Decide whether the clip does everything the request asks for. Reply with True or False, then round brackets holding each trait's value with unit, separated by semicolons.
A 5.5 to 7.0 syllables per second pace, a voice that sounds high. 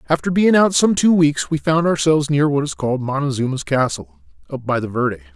False (6.0 syllables/s; 150 Hz)